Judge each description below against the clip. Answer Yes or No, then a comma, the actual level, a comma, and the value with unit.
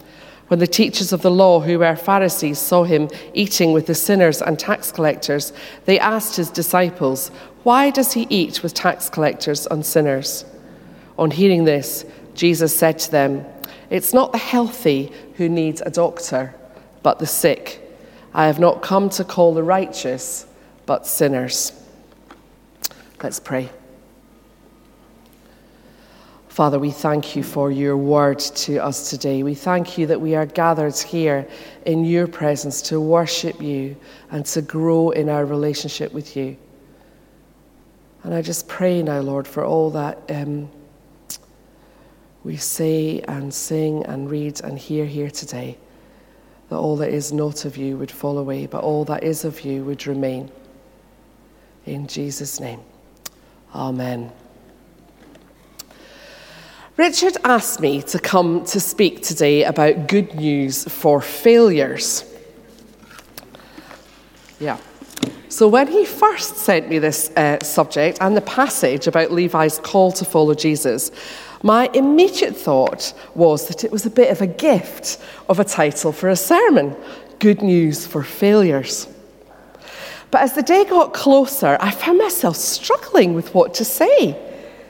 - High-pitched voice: No, medium, 160 Hz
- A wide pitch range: No, average, 4.7 semitones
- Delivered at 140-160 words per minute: Yes, average, 145 wpm